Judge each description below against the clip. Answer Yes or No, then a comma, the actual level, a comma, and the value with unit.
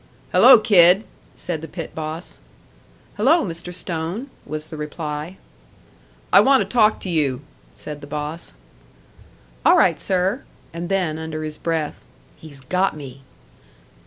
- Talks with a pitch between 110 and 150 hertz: No, medium, 165 Hz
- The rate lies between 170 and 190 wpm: No, slow, 135 wpm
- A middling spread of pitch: Yes, average, 3.6 semitones